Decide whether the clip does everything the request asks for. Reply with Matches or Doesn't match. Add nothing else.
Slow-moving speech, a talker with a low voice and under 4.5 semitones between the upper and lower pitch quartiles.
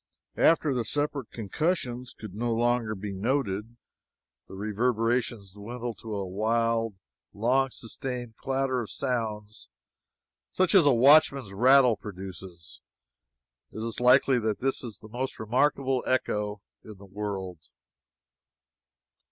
Matches